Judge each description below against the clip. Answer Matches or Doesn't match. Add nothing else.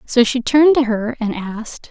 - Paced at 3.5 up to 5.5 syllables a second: Matches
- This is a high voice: Matches